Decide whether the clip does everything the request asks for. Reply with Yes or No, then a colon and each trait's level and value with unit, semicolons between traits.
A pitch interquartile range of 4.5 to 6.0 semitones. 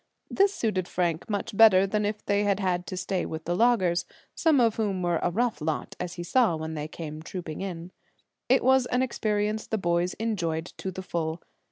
No: average, 4.1 semitones